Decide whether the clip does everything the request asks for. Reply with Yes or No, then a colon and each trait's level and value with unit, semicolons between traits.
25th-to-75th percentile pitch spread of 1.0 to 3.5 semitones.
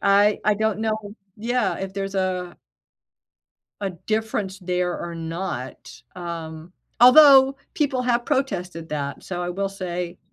No: average, 3.9 semitones